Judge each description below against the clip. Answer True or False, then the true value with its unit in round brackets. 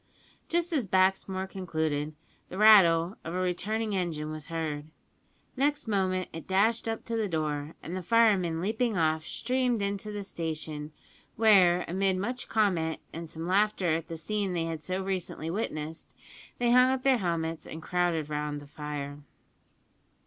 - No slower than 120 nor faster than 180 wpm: True (160 wpm)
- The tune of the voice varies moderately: True (4.8 semitones)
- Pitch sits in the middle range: True (180 Hz)